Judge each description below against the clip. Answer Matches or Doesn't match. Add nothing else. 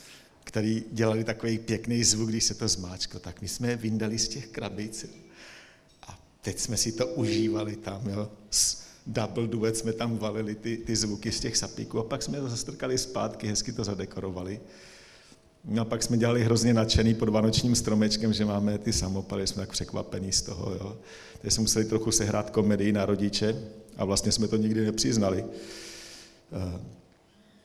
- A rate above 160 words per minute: Matches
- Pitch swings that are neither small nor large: Doesn't match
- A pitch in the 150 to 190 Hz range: Doesn't match